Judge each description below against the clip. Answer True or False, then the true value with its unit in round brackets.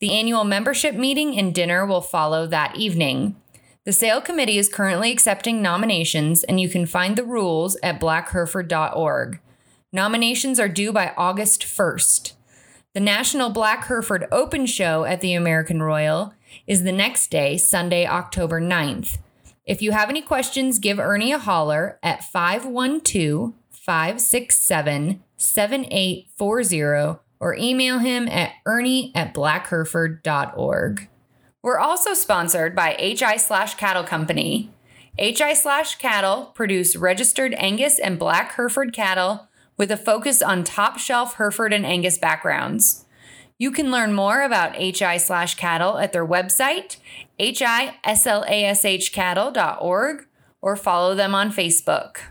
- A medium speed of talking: False (130 wpm)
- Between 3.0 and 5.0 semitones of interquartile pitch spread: False (5.4 semitones)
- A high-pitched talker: True (200 Hz)